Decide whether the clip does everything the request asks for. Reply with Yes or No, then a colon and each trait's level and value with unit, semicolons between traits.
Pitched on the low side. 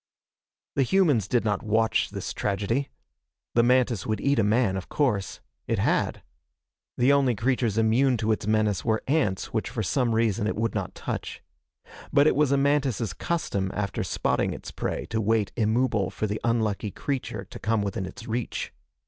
Yes: low, 115 Hz